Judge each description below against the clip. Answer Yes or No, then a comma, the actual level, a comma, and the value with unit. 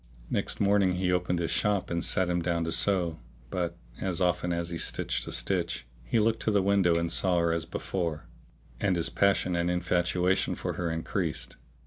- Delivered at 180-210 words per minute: Yes, average, 190 wpm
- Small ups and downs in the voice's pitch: Yes, narrow, 2.0 semitones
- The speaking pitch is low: Yes, very low, 90 Hz